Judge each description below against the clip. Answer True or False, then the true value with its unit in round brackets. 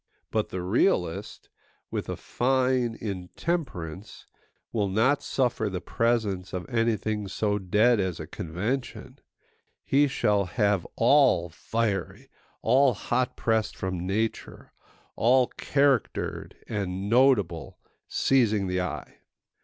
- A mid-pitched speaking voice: False (110 Hz)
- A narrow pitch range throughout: False (4.8 semitones)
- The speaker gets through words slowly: True (110 wpm)